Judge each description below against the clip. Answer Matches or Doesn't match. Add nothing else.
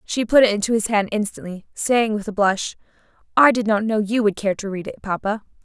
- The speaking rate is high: Matches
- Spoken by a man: Doesn't match